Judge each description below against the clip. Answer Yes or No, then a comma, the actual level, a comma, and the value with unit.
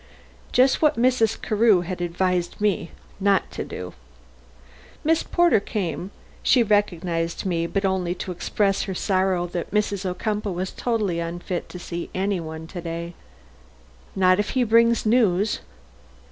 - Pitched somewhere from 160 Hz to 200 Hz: Yes, high, 190 Hz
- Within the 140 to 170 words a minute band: Yes, average, 145 wpm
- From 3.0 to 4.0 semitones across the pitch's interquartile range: Yes, average, 3.5 semitones